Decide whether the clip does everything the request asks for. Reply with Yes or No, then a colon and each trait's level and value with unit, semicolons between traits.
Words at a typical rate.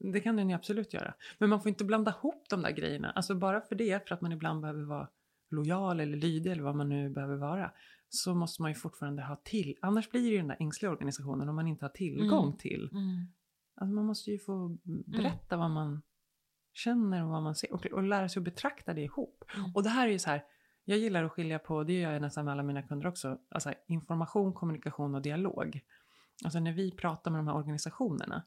No: fast, 230 wpm